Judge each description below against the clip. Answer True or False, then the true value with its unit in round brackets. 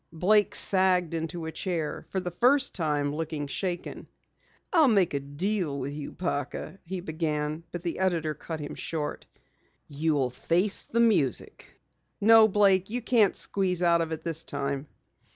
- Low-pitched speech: False (170 Hz)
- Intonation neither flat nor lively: True (4.1 semitones)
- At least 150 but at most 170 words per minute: True (155 wpm)